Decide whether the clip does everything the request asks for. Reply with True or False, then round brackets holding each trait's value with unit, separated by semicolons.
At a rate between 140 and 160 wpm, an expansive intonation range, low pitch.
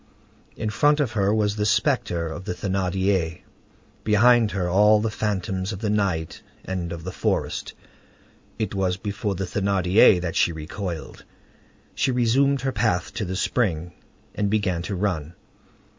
False (155 wpm; 3.3 semitones; 100 Hz)